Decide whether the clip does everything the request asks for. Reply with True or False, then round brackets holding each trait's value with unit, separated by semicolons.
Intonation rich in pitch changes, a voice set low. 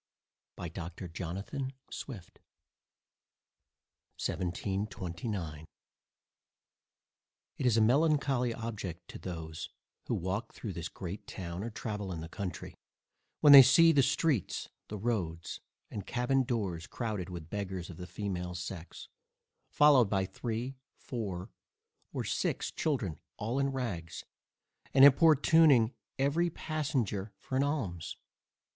True (6.9 semitones; 105 Hz)